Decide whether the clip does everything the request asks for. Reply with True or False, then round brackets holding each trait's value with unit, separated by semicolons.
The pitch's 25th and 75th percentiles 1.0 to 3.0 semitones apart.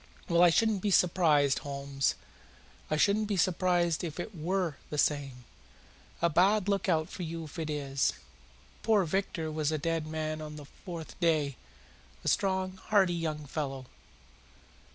False (3.5 semitones)